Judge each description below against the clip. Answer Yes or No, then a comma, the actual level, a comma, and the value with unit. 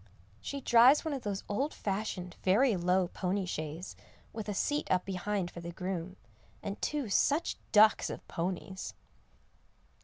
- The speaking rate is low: No, average, 150 wpm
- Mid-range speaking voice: No, high, 195 Hz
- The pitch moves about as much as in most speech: Yes, average, 4.2 semitones